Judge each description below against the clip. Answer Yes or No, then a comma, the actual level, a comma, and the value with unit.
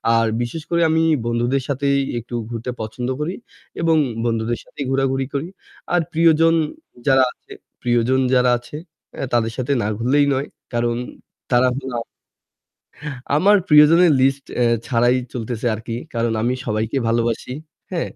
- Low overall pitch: Yes, low, 125 Hz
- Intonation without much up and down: No, average, 3.3 semitones